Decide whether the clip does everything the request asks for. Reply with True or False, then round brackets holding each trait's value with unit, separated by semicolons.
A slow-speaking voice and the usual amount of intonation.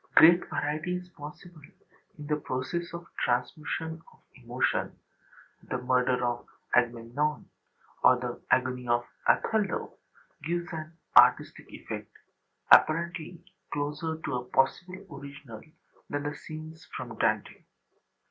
True (115 wpm; 4.6 semitones)